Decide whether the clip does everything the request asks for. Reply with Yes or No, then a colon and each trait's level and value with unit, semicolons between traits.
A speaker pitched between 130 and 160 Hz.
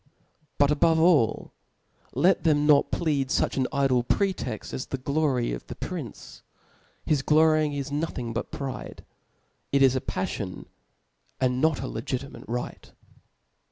Yes: medium, 140 Hz